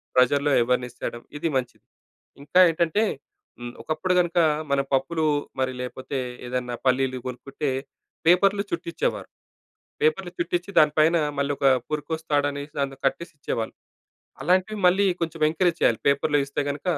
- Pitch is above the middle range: No, medium, 145 Hz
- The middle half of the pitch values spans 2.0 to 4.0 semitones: No, average, 4.7 semitones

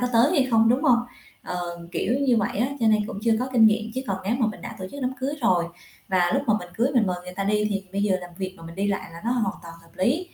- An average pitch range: Yes, average, 4.6 semitones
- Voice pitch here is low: No, high, 215 Hz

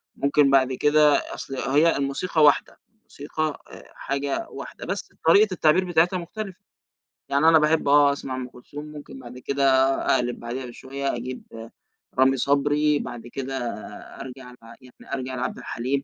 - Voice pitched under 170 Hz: Yes, medium, 140 Hz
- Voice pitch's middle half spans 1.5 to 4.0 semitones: Yes, average, 2.7 semitones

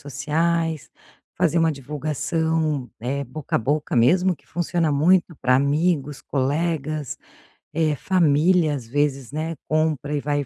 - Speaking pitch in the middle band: Yes, medium, 150 Hz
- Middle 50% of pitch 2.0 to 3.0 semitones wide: Yes, narrow, 2.6 semitones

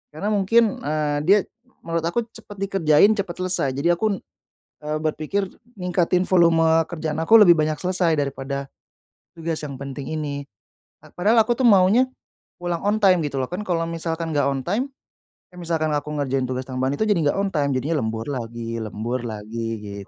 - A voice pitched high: No, medium, 160 Hz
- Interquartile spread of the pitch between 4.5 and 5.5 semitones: Yes, average, 5.1 semitones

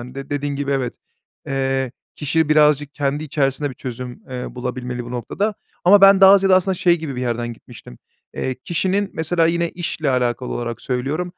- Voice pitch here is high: No, medium, 140 Hz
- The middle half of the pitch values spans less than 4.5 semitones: No, average, 5.2 semitones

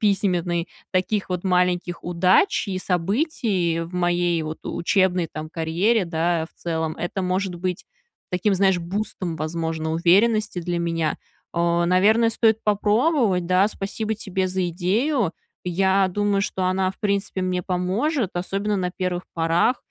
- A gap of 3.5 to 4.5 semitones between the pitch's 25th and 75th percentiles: No, average, 2.7 semitones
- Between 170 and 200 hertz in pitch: Yes, medium, 185 Hz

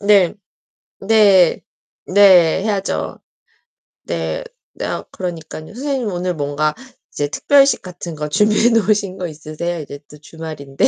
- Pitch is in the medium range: Yes, medium, 180 Hz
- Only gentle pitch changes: No, average, 5.1 semitones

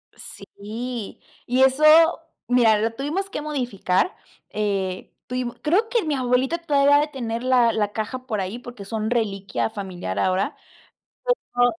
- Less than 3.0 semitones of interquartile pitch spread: No, average, 4.8 semitones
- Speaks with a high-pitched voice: Yes, high, 245 Hz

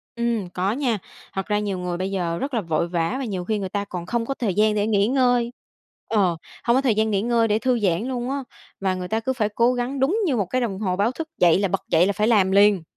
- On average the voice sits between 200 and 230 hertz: Yes, high, 210 Hz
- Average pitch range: Yes, average, 4.1 semitones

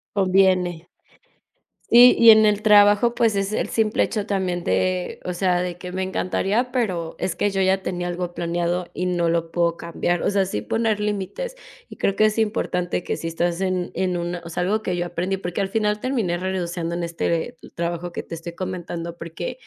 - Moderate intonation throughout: Yes, average, 3.0 semitones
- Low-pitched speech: No, medium, 185 Hz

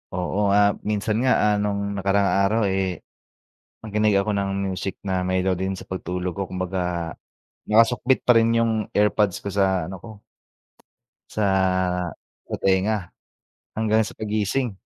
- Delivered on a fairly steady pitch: Yes, narrow, 2.3 semitones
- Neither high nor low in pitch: No, low, 100 Hz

